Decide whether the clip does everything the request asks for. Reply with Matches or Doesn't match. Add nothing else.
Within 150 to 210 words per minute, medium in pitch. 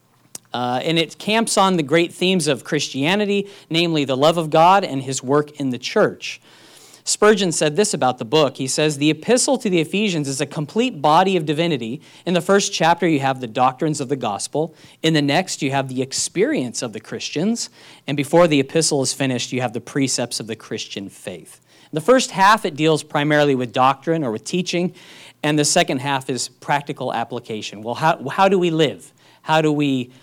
Matches